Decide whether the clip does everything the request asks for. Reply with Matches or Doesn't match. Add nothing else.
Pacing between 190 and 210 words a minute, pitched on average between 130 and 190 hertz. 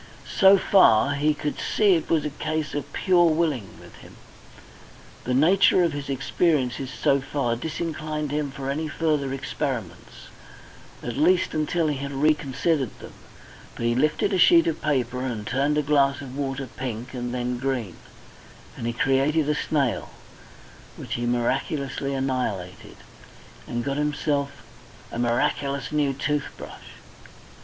Doesn't match